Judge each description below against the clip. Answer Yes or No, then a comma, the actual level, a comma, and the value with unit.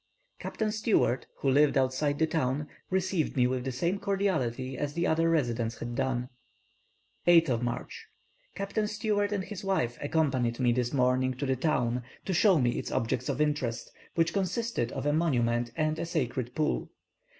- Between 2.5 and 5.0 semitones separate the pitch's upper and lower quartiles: No, wide, 5.4 semitones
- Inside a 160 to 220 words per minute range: Yes, average, 170 wpm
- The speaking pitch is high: No, medium, 145 Hz